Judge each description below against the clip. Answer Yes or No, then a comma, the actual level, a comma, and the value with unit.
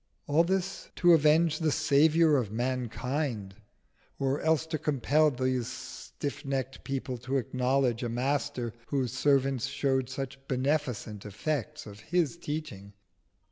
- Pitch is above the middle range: No, low, 135 Hz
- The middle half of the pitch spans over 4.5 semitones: No, average, 3.3 semitones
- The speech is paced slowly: Yes, slow, 130 wpm